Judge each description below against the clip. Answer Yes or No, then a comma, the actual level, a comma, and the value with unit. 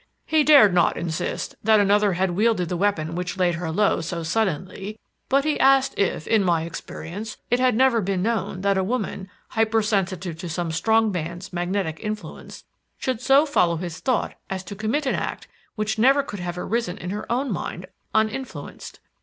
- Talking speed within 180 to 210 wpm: Yes, average, 185 wpm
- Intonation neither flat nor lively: Yes, average, 4.2 semitones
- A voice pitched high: Yes, high, 200 Hz